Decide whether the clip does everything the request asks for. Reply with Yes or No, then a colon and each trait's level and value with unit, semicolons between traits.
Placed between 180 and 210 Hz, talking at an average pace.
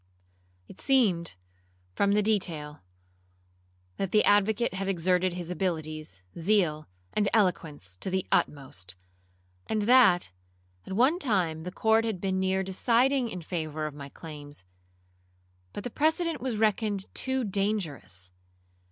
No: high, 190 Hz; slow, 130 wpm